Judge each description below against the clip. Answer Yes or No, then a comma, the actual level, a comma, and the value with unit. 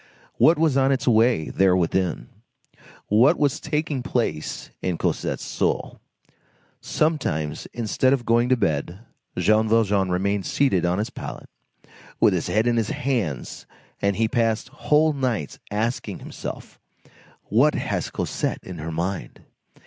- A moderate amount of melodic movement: No, wide, 5.8 semitones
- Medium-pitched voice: No, low, 110 Hz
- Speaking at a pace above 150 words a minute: No, average, 140 wpm